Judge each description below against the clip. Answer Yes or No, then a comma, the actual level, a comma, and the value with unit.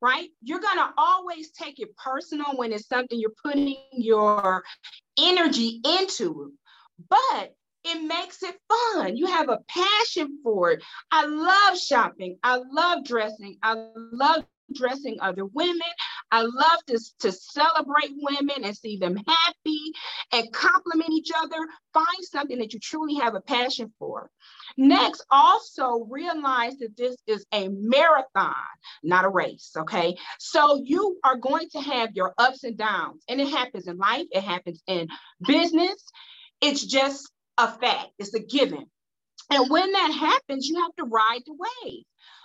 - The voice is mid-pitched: No, very high, 275 Hz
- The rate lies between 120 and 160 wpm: Yes, average, 155 wpm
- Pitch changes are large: Yes, wide, 6.4 semitones